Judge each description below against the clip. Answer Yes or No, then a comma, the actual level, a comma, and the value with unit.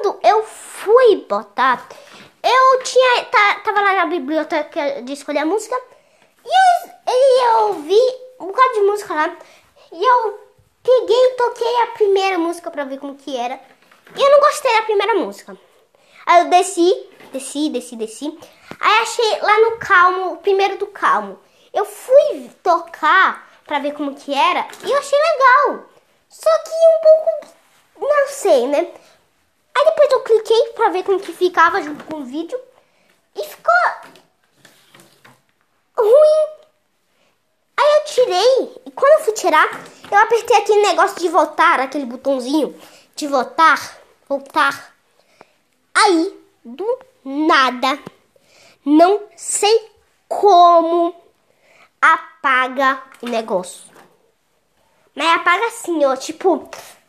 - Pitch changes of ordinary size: No, wide, 6.4 semitones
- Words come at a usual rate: Yes, average, 130 wpm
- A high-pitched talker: Yes, very high, 350 Hz